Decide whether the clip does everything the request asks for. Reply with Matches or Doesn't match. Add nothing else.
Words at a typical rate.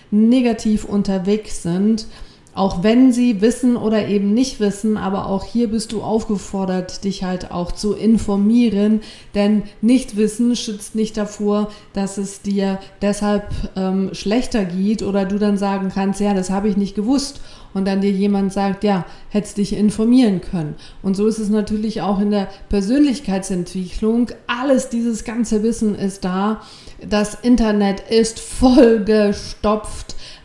Matches